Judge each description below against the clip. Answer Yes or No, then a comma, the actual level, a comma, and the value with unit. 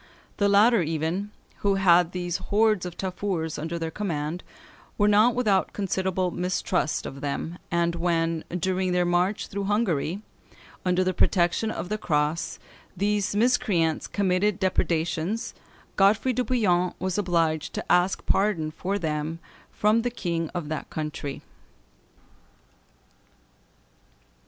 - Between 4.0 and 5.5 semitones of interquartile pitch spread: No, average, 3.5 semitones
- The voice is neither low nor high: Yes, medium, 180 Hz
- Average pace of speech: No, slow, 125 wpm